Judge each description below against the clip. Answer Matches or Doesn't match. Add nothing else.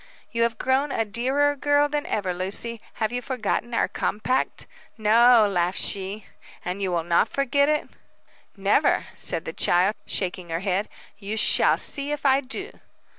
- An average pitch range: Doesn't match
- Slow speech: Doesn't match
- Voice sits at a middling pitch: Doesn't match